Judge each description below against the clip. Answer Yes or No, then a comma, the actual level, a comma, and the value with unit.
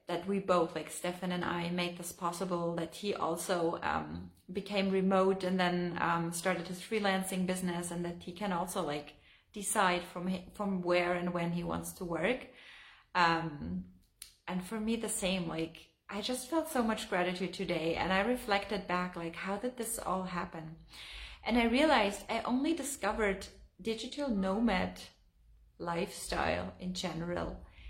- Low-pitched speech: No, medium, 180 Hz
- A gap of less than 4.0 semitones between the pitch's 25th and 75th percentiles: Yes, average, 2.9 semitones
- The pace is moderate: Yes, average, 160 wpm